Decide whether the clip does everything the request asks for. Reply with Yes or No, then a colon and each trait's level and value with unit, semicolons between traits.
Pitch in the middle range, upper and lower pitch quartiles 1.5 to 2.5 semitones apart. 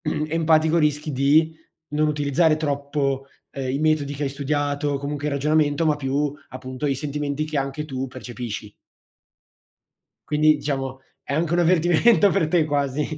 Yes: medium, 145 Hz; narrow, 1.9 semitones